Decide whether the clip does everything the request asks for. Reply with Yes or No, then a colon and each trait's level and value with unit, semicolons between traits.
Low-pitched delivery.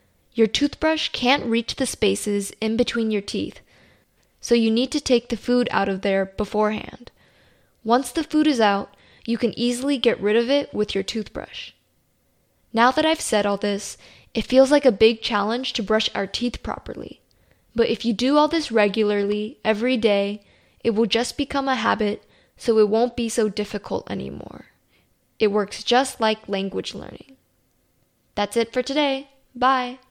No: high, 230 Hz